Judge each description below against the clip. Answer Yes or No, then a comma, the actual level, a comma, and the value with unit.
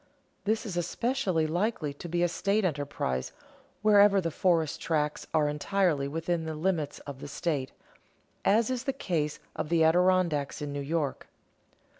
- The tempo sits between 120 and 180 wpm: Yes, average, 155 wpm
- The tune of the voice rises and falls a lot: No, average, 4.3 semitones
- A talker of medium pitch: Yes, medium, 165 Hz